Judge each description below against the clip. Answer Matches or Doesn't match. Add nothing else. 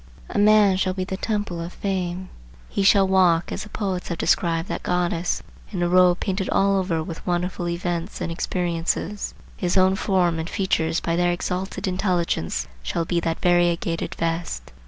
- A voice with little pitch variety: Matches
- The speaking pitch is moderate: Matches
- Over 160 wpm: Matches